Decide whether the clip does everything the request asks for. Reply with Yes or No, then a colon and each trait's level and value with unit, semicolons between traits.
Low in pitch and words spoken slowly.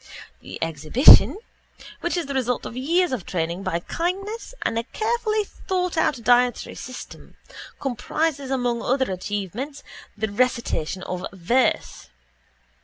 No: very high, 255 Hz; slow, 120 wpm